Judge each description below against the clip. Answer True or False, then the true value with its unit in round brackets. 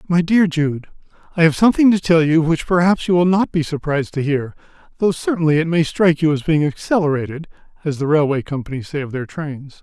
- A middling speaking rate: False (210 wpm)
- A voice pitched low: False (160 Hz)